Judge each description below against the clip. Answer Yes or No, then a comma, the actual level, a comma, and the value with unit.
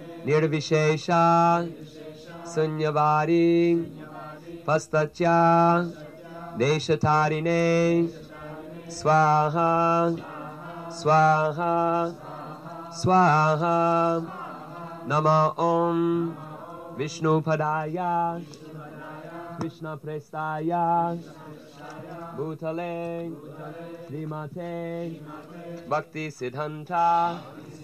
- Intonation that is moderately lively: No, narrow, 1.6 semitones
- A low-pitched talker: No, medium, 160 Hz